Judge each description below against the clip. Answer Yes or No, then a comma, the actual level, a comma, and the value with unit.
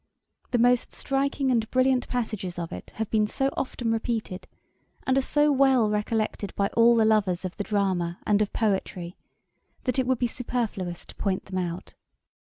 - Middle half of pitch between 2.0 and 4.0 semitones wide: No, average, 4.5 semitones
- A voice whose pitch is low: No, high, 220 Hz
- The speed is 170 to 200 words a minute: Yes, average, 175 wpm